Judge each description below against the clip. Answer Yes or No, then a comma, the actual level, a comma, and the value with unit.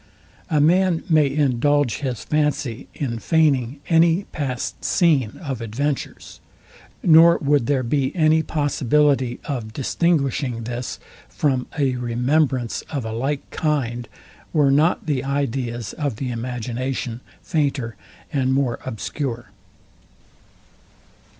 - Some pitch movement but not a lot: Yes, average, 3.6 semitones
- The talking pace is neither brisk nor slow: No, slow, 110 wpm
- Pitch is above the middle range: No, low, 135 Hz